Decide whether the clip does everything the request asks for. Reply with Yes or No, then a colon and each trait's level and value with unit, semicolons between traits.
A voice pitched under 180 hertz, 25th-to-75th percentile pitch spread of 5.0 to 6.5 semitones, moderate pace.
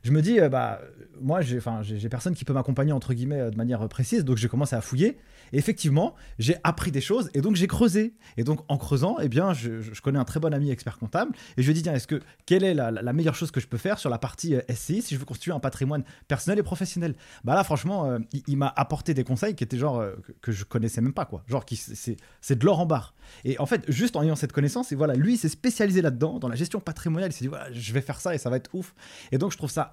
No: medium, 140 Hz; average, 5.3 semitones; fast, 300 wpm